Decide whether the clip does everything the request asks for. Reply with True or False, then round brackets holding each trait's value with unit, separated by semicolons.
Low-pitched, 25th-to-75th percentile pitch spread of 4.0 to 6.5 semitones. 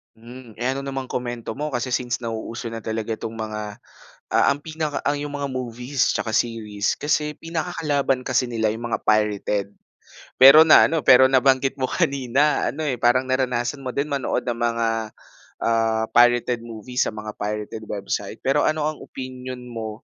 False (125 Hz; 3.5 semitones)